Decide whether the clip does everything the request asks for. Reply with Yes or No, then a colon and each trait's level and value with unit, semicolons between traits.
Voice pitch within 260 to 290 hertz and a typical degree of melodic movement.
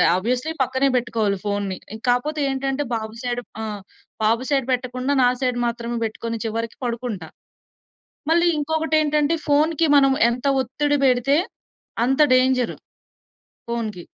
No: very high, 250 Hz; average, 3.6 semitones